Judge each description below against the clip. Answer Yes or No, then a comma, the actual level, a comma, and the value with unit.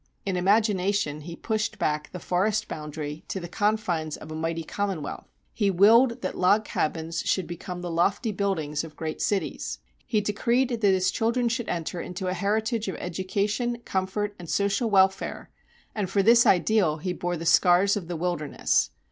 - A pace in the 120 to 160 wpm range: No, average, 175 wpm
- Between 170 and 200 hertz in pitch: Yes, high, 190 Hz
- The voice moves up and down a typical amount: Yes, average, 3.9 semitones